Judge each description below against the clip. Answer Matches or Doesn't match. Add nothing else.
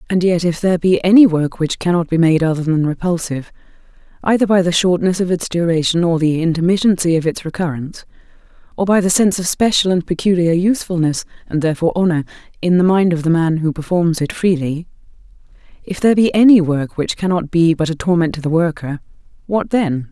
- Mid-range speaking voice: Matches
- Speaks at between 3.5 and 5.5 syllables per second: Doesn't match